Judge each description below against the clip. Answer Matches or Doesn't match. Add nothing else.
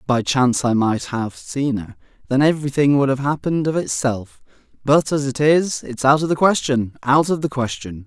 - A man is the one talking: Matches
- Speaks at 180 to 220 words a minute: Matches